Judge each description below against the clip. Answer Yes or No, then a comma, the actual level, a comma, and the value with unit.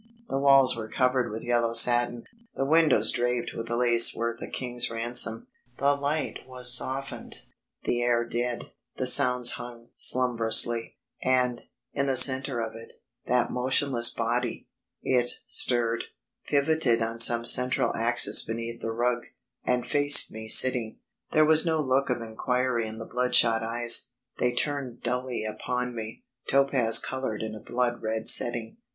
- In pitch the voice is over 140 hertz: No, low, 120 Hz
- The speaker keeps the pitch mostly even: Yes, narrow, 1.9 semitones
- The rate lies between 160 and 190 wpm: No, average, 150 wpm